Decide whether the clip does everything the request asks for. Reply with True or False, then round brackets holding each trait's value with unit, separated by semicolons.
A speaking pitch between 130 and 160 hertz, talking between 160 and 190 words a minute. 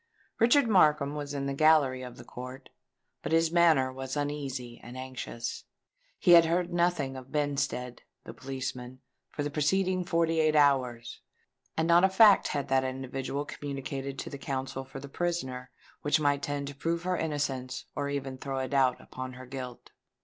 True (140 Hz; 170 wpm)